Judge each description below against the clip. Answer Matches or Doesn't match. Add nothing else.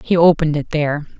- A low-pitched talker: Doesn't match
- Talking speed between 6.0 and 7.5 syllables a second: Matches